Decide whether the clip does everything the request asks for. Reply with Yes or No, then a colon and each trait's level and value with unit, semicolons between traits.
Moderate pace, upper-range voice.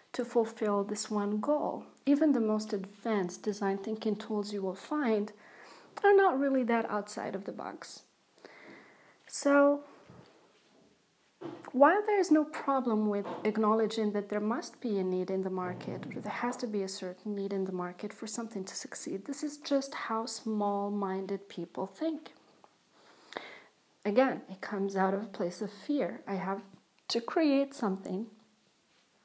Yes: average, 160 wpm; high, 215 Hz